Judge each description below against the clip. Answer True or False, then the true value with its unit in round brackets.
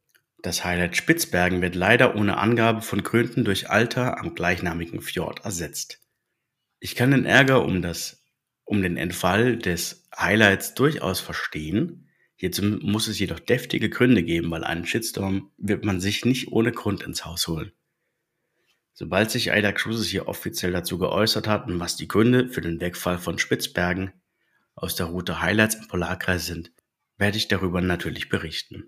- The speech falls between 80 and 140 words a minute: False (160 wpm)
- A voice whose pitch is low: True (95 Hz)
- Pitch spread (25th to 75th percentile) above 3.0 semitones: True (3.7 semitones)